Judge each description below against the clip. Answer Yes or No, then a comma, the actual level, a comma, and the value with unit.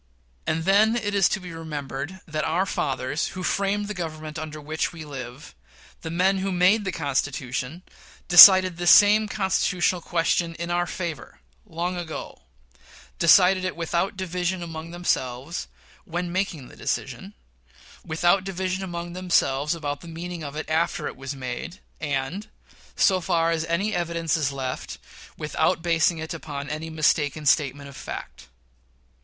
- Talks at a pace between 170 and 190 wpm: No, average, 150 wpm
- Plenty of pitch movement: No, average, 3.3 semitones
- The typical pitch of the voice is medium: Yes, medium, 170 Hz